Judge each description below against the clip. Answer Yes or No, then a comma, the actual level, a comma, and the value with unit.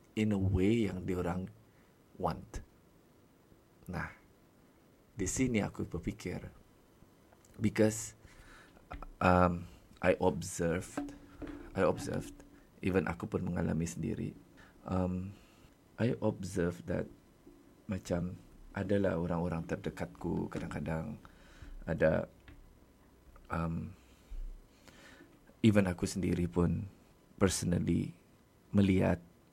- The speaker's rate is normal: No, slow, 80 wpm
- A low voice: Yes, very low, 90 Hz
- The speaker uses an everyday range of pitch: Yes, average, 3.0 semitones